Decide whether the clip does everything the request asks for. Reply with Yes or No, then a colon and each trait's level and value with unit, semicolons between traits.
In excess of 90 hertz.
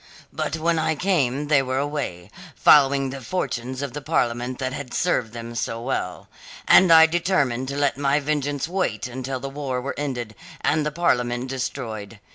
Yes: low, 135 Hz